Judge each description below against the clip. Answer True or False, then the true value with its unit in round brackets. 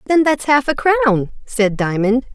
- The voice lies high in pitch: True (240 Hz)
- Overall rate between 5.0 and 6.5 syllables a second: False (4.1 syllables/s)